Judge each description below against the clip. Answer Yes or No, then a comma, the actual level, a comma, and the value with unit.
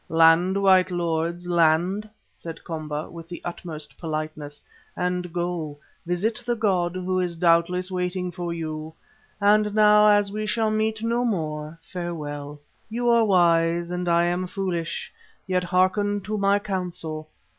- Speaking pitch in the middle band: Yes, medium, 180 Hz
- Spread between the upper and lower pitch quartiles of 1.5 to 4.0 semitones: Yes, average, 3.3 semitones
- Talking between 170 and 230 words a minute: No, average, 145 wpm